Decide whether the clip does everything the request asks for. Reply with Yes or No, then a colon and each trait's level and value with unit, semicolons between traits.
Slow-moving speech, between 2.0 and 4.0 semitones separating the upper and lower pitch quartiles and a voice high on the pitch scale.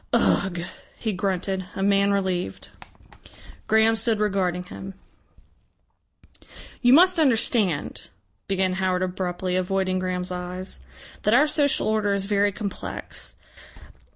Yes: slow, 110 wpm; narrow, 2.6 semitones; high, 195 Hz